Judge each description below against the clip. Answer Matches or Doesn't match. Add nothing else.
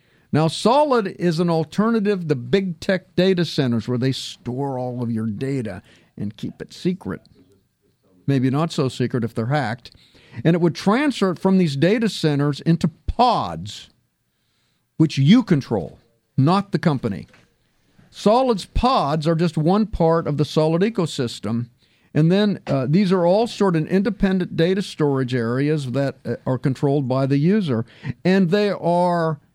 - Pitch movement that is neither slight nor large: Doesn't match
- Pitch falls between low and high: Matches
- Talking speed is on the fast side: Doesn't match